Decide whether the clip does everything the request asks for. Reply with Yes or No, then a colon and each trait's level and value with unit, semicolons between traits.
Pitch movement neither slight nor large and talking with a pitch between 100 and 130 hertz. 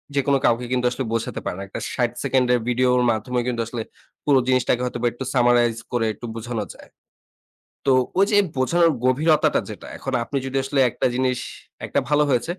No: narrow, 1.9 semitones; low, 125 Hz